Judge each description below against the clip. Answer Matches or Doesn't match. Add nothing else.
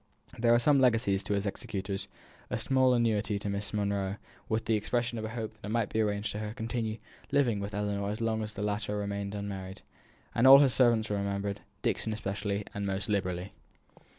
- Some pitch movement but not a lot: Doesn't match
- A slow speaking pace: Doesn't match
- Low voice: Matches